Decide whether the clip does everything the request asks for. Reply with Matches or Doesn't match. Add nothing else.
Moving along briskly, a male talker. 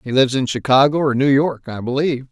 Matches